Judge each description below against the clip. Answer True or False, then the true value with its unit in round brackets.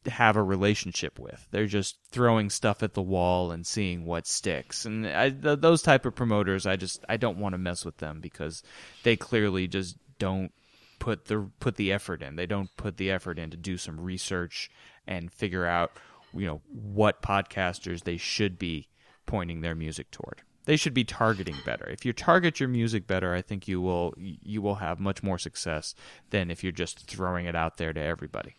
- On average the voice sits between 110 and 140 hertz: False (95 Hz)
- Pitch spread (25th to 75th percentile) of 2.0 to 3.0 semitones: False (3.6 semitones)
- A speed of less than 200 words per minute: False (205 wpm)